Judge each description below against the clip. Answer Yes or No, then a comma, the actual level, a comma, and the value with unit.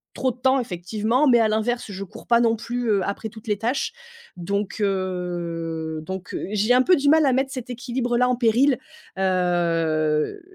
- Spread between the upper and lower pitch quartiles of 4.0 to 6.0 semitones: Yes, average, 5.3 semitones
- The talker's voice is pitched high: Yes, high, 220 Hz